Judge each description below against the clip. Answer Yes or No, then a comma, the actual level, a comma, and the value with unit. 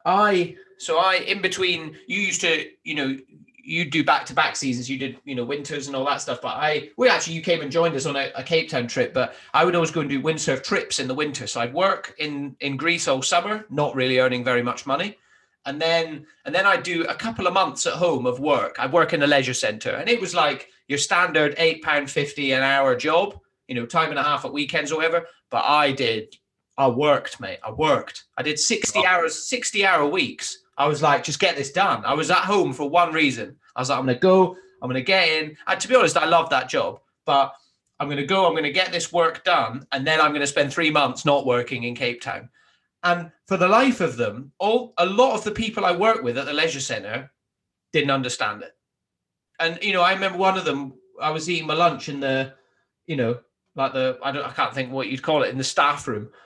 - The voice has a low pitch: No, medium, 155 Hz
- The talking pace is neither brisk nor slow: No, fast, 250 wpm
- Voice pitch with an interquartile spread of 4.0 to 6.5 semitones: Yes, average, 4.6 semitones